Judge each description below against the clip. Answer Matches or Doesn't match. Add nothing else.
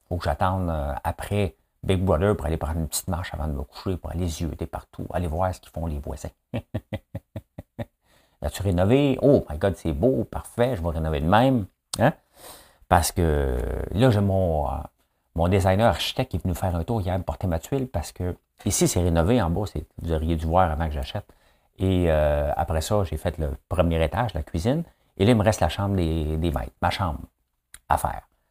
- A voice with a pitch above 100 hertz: Doesn't match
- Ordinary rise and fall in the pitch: Matches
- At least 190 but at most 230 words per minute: Matches